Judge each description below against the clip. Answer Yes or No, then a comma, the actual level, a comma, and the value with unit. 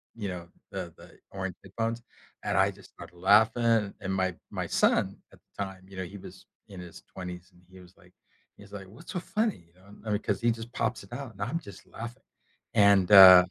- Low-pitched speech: Yes, low, 100 Hz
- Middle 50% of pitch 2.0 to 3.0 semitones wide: No, average, 3.4 semitones